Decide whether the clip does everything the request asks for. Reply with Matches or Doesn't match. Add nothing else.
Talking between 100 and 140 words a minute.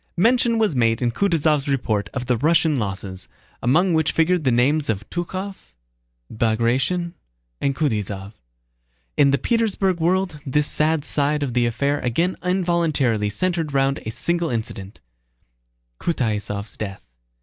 Matches